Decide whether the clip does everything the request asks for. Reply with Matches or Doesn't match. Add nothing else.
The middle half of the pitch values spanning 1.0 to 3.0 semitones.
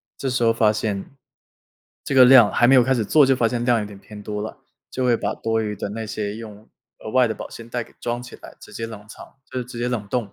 Matches